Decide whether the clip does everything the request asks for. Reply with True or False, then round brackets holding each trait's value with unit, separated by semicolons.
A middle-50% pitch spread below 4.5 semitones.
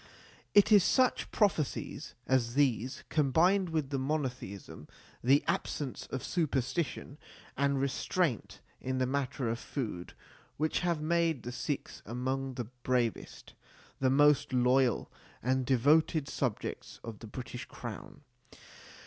True (3.5 semitones)